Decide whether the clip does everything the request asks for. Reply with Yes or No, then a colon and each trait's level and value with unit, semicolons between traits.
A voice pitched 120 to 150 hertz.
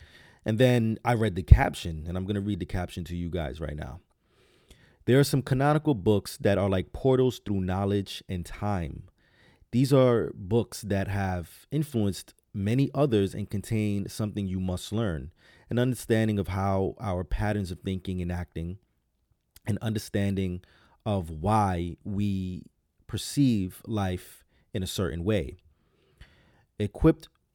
No: low, 100 Hz